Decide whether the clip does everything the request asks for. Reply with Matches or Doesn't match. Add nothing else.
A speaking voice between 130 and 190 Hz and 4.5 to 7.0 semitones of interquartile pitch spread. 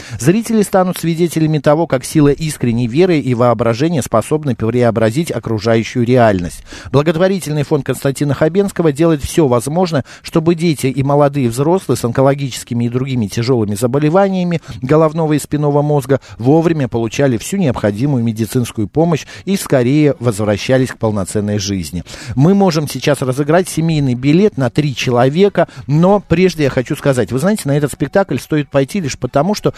Matches